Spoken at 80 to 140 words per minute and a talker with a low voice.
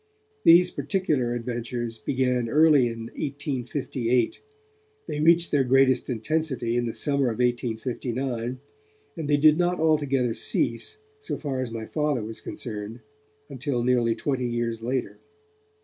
Yes: slow, 135 wpm; low, 125 Hz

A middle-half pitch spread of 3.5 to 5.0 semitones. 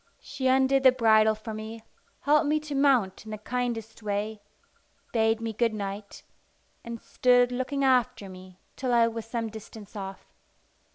No: average, 2.9 semitones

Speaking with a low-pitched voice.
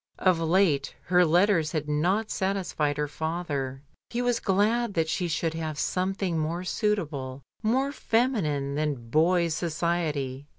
No: medium, 165 Hz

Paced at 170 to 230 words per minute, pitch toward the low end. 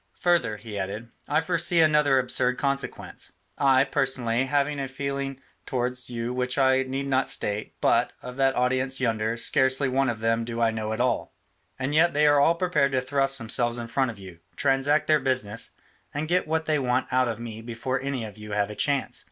Yes: average, 200 wpm; low, 130 Hz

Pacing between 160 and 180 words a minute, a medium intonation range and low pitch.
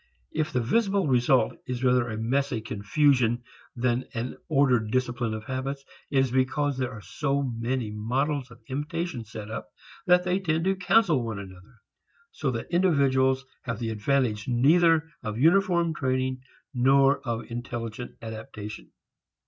No: average, 150 wpm; average, 3.7 semitones; low, 130 Hz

